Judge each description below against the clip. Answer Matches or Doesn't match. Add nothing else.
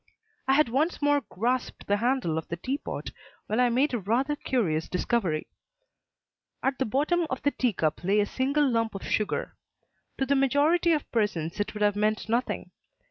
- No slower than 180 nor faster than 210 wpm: Matches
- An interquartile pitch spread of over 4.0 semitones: Matches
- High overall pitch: Matches